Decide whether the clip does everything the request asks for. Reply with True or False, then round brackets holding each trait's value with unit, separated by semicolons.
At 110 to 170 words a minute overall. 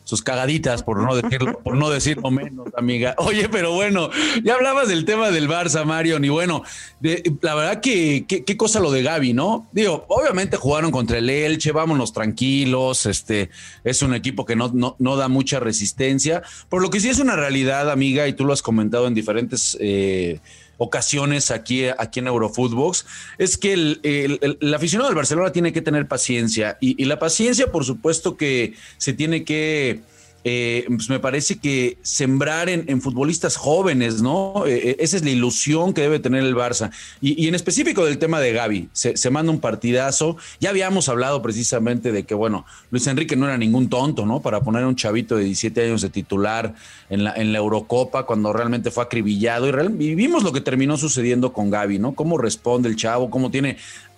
False (200 wpm)